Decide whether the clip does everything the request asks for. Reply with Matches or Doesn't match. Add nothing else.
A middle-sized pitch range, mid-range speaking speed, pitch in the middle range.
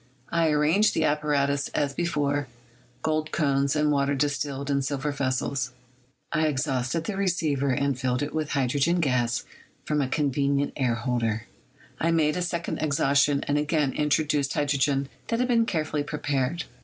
Doesn't match